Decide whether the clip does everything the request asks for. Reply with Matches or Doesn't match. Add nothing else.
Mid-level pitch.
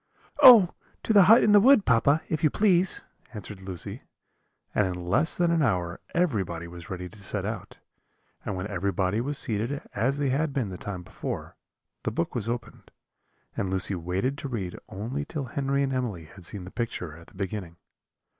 Doesn't match